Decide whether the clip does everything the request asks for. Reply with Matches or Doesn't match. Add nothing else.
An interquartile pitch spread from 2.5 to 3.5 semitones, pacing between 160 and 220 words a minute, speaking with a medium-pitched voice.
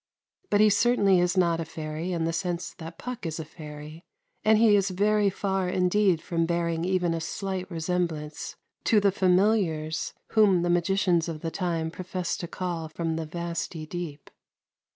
Matches